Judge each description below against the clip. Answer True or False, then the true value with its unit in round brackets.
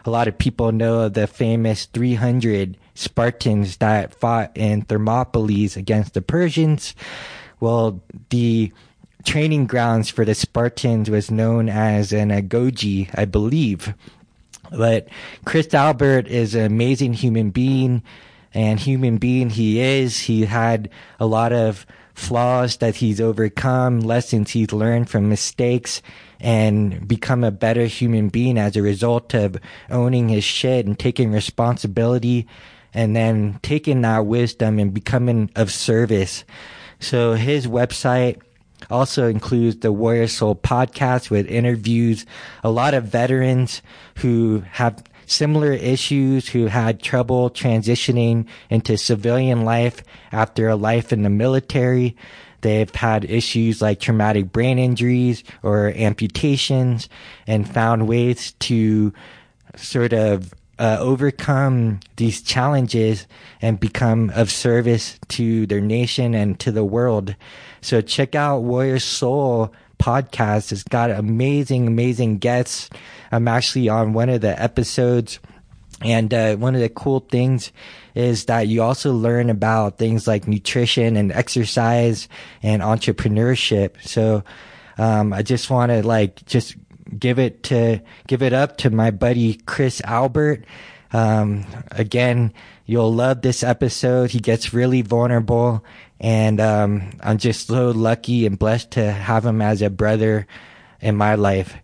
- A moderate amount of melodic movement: False (2.3 semitones)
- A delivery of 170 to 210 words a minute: False (135 wpm)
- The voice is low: True (115 Hz)